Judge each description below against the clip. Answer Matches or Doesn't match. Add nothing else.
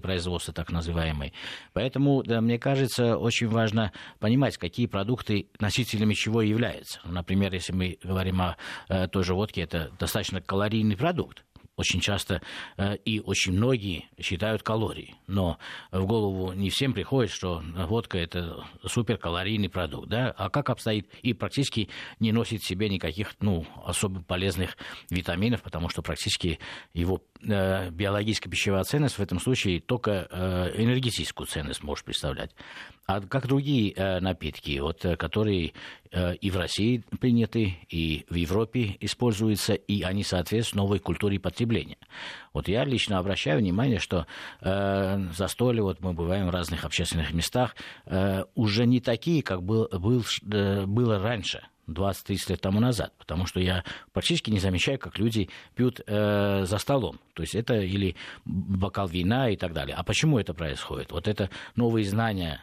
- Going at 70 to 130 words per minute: Doesn't match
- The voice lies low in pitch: Matches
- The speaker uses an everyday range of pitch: Matches